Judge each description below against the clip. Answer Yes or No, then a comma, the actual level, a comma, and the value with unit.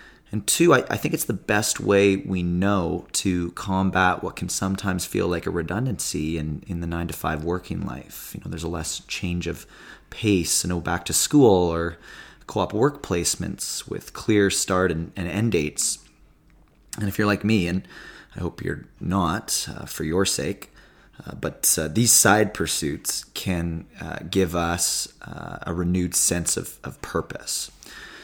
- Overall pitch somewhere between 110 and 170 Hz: No, very low, 90 Hz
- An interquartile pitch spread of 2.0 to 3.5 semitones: Yes, average, 2.8 semitones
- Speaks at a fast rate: No, average, 180 wpm